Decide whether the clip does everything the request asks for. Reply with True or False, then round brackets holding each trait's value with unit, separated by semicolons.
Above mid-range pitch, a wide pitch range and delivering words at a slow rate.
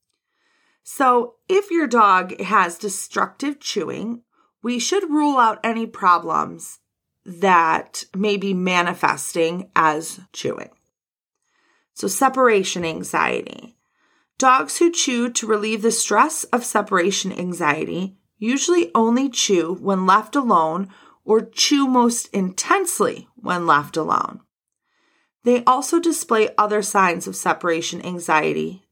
True (210 Hz; 6.0 semitones; 110 wpm)